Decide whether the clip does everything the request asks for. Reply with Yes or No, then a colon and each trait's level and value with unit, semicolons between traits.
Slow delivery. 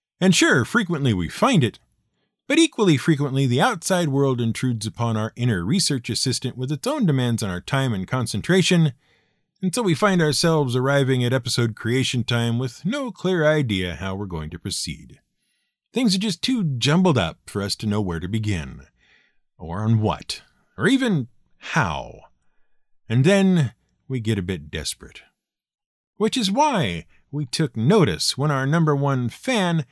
No: average, 165 wpm